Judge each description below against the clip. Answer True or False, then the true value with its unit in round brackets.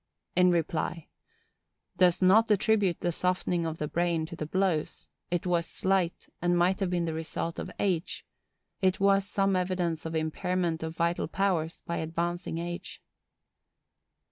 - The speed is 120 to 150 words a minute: True (145 wpm)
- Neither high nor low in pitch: True (175 Hz)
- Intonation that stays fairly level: True (2.0 semitones)